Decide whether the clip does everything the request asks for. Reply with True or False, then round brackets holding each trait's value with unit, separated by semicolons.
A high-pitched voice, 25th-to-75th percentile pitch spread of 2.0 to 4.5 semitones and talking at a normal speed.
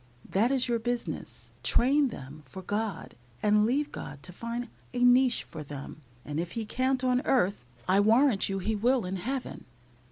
False (225 Hz; 4.9 semitones; 180 wpm)